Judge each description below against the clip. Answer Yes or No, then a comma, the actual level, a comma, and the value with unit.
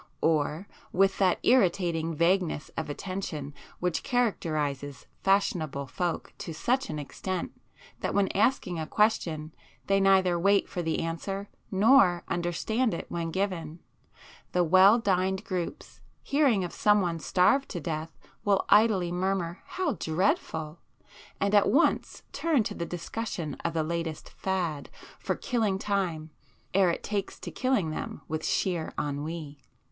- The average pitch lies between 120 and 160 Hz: No, medium, 180 Hz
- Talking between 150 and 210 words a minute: No, average, 140 wpm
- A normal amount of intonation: Yes, average, 3.7 semitones